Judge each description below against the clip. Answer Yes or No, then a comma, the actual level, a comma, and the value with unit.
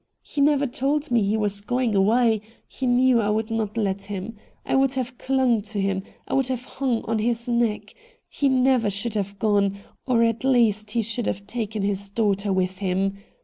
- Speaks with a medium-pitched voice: No, high, 225 Hz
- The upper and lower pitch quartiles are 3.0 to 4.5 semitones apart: Yes, average, 3.7 semitones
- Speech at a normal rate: No, fast, 215 wpm